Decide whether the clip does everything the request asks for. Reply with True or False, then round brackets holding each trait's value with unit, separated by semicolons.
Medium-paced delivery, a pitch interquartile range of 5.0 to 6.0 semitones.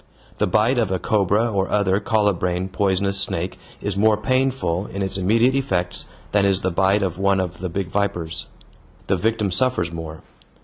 False (175 wpm; 2.7 semitones)